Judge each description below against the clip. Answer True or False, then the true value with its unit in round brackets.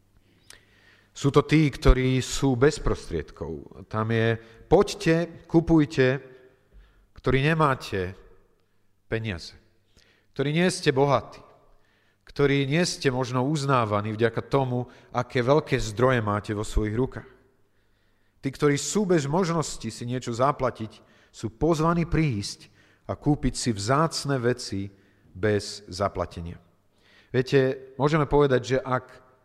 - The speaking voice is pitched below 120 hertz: False (125 Hz)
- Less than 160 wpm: True (110 wpm)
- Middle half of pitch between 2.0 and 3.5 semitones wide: False (5.2 semitones)